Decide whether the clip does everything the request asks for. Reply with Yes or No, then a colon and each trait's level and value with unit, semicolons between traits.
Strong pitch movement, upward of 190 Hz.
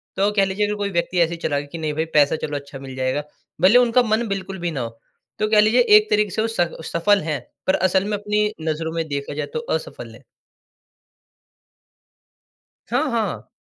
No: wide, 5.7 semitones; medium, 185 Hz